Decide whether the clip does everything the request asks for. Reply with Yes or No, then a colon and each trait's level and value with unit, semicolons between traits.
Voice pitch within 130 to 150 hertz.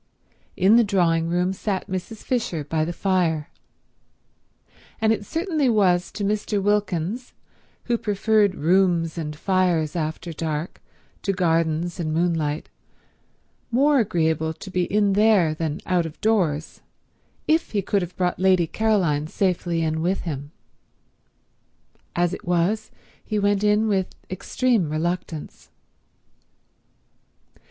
No: medium, 180 Hz